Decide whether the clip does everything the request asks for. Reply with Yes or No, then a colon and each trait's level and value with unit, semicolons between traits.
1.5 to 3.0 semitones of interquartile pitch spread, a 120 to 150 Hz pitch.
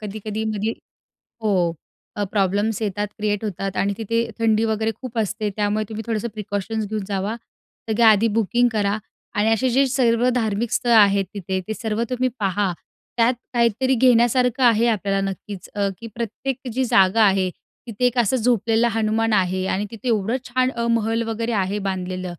No: narrow, 2.4 semitones; high, 220 Hz